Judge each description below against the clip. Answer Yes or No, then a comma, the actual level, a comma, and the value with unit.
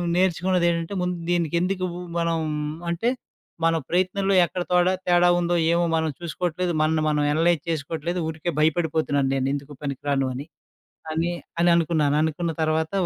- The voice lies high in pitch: No, medium, 170 Hz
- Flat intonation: Yes, narrow, 2.0 semitones